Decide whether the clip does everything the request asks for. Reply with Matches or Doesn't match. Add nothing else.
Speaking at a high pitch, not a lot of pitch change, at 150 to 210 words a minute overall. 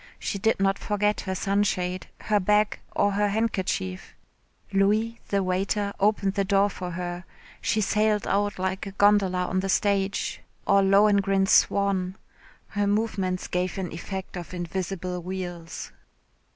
Doesn't match